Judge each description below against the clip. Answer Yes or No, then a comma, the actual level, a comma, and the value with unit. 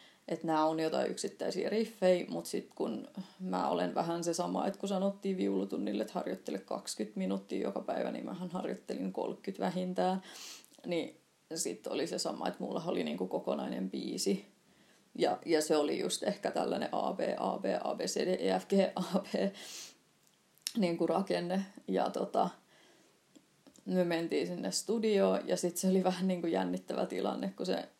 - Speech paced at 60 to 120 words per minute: No, average, 150 wpm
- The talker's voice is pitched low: No, medium, 175 Hz